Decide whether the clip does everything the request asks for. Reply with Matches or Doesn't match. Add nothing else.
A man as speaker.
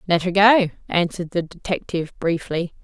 Doesn't match